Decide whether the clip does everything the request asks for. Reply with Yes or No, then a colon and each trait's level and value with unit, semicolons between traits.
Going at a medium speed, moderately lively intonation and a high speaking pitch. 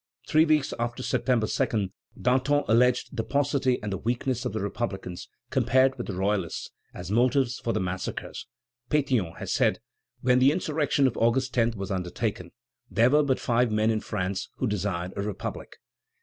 No: average, 170 wpm; average, 4.5 semitones; low, 120 Hz